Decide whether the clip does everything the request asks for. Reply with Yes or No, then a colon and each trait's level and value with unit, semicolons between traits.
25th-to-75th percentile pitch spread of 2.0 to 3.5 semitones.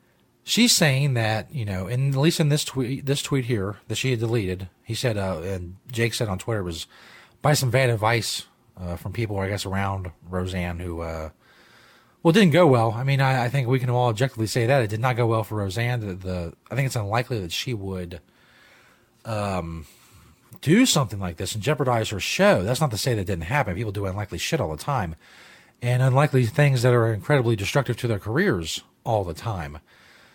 No: wide, 5.4 semitones